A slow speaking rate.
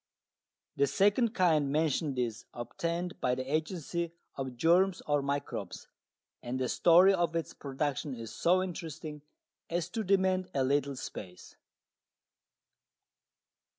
Yes: slow, 120 wpm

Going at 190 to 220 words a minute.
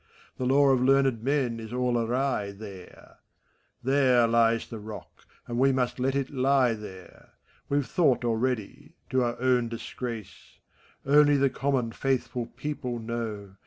No: average, 145 wpm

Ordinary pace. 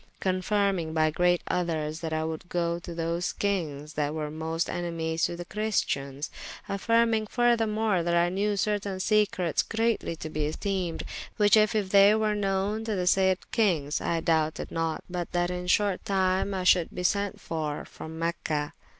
Yes: average, 165 wpm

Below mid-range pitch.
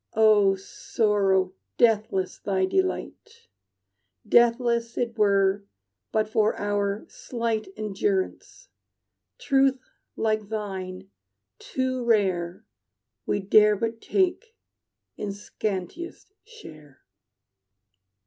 No: high, 215 Hz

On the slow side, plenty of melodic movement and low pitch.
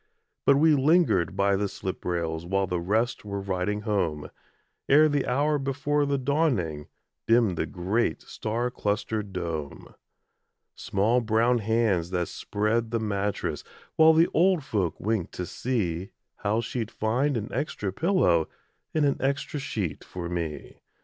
No: average, 145 wpm; wide, 6.7 semitones; low, 110 Hz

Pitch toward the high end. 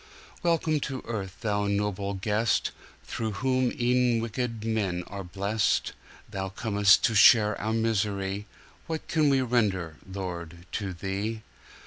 No: low, 105 Hz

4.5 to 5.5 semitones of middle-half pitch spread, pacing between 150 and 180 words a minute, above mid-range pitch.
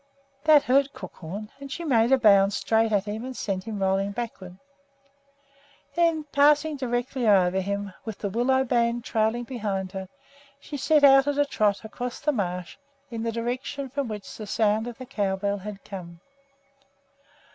Yes: average, 4.8 semitones; average, 170 wpm; high, 225 Hz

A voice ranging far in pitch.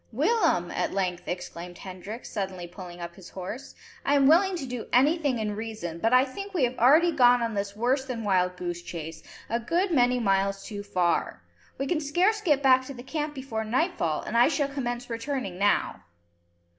Yes: wide, 6.6 semitones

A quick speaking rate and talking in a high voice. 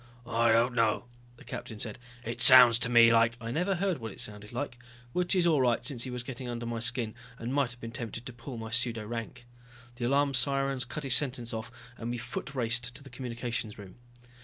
No: fast, 225 wpm; low, 120 Hz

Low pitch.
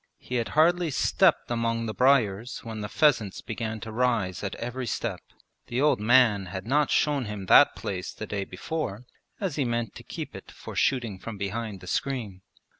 Yes: low, 115 Hz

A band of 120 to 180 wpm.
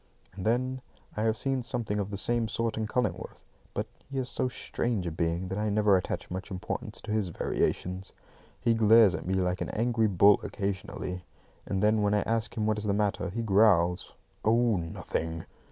No: average, 200 wpm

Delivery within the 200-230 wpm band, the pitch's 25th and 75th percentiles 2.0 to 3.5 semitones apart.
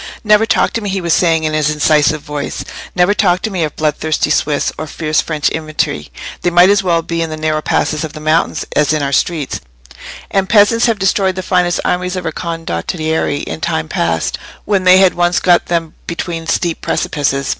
Yes: fast, 205 wpm; average, 3.1 semitones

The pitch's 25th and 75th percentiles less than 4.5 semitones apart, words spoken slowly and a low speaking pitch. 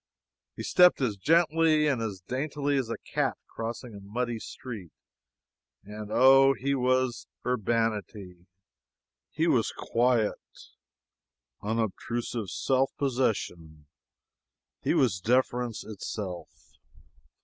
Yes: average, 4.0 semitones; slow, 100 wpm; low, 120 Hz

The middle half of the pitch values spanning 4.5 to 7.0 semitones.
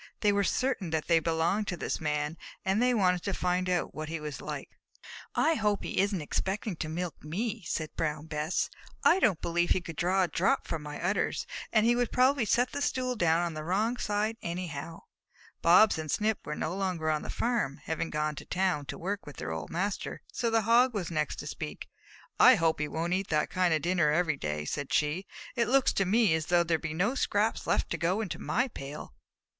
Yes: average, 4.9 semitones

